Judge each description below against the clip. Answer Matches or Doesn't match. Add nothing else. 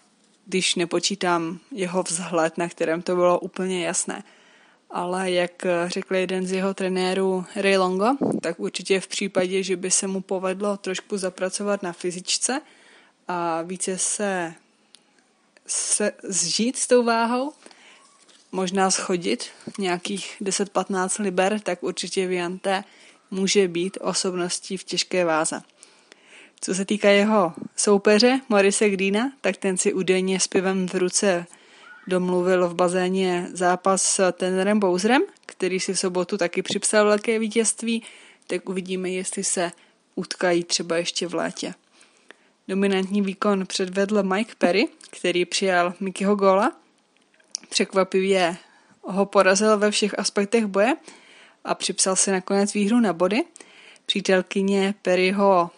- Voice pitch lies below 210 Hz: Matches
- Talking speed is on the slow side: Doesn't match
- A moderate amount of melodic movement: Doesn't match